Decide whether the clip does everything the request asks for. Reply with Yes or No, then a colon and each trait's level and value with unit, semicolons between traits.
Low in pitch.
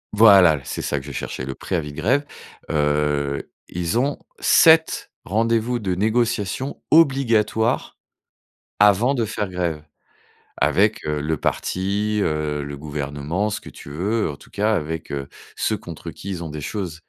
Yes: very low, 95 Hz